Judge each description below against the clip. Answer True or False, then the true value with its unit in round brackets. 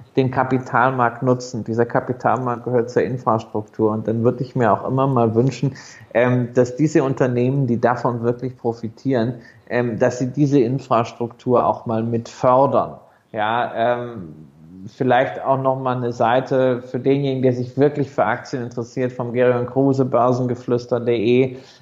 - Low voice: True (125 Hz)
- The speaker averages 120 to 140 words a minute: True (135 wpm)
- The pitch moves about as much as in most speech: False (1.8 semitones)